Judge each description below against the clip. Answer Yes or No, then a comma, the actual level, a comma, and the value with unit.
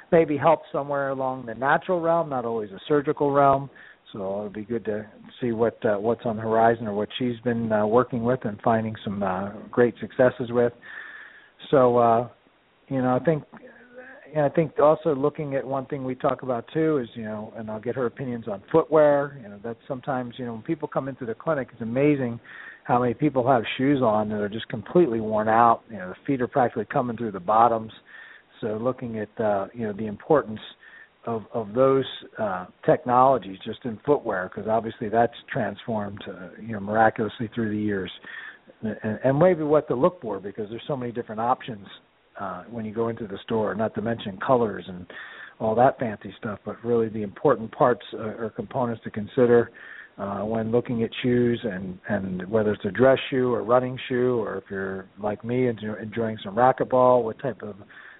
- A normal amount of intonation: Yes, average, 3.6 semitones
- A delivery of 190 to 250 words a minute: Yes, average, 200 wpm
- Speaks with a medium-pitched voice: No, low, 120 Hz